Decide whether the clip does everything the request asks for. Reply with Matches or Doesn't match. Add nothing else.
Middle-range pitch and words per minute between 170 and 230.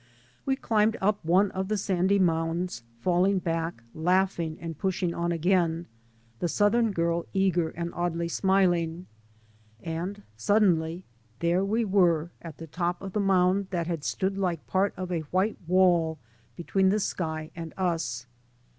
Doesn't match